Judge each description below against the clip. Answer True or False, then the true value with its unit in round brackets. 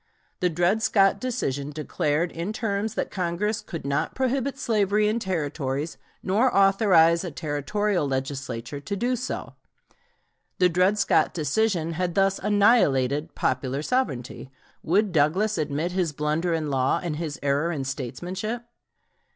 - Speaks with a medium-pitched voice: True (175 Hz)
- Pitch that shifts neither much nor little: False (5.9 semitones)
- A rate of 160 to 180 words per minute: False (135 wpm)